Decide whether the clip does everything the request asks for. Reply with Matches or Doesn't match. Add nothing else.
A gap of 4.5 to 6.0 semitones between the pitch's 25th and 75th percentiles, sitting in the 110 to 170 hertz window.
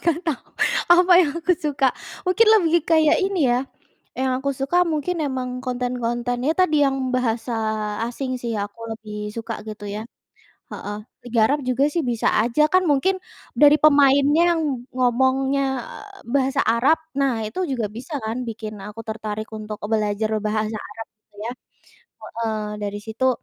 Doesn't match